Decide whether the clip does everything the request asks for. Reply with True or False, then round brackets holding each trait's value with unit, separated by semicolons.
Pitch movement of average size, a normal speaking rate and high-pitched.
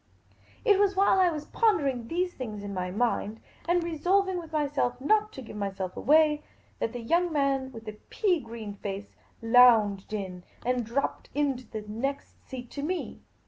False (7.3 semitones; 175 wpm; 260 Hz)